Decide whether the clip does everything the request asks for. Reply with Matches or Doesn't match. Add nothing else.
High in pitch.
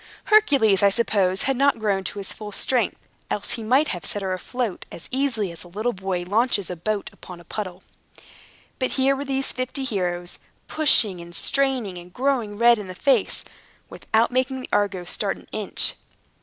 Matches